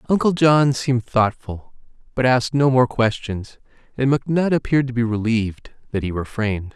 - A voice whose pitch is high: No, low, 125 Hz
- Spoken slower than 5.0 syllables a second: No, 5.5 syllables/s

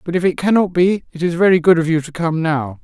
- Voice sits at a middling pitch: Yes, medium, 170 Hz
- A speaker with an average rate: No, fast, 295 wpm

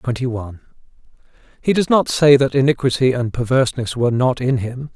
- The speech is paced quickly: No, average, 170 wpm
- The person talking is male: Yes, male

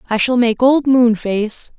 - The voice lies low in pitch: No, high, 240 Hz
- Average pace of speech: Yes, average, 170 wpm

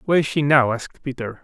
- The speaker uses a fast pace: Yes, fast, 250 wpm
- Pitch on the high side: No, low, 135 Hz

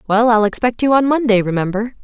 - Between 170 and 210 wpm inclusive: Yes, fast, 205 wpm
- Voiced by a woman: Yes, female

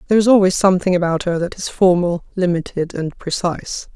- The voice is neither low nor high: Yes, medium, 180 Hz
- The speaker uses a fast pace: No, average, 180 wpm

